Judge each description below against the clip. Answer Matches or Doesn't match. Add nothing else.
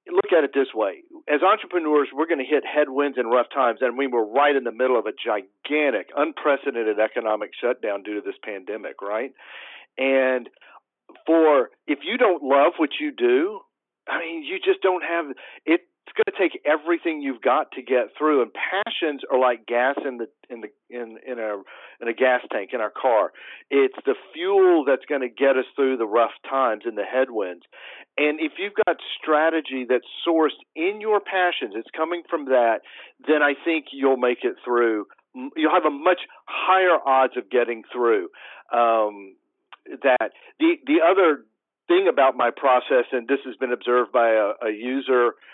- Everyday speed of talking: Matches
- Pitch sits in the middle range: Matches